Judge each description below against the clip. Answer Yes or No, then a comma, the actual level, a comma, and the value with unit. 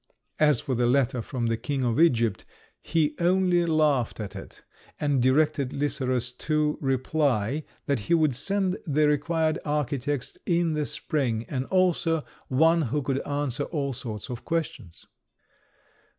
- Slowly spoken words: No, average, 145 wpm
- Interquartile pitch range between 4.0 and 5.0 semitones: No, average, 3.6 semitones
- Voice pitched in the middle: Yes, medium, 145 Hz